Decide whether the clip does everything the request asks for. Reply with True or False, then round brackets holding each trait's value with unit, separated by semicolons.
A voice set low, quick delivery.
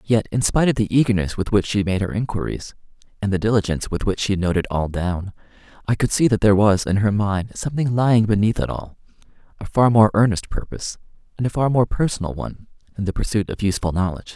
True (105 Hz; 215 wpm)